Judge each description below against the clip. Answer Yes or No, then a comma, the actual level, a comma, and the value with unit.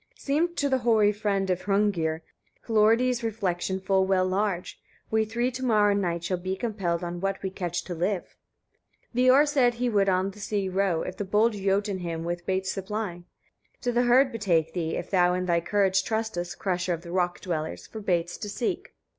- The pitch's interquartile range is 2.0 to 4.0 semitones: Yes, average, 3.6 semitones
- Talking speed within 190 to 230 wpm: Yes, fast, 205 wpm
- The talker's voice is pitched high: Yes, high, 195 Hz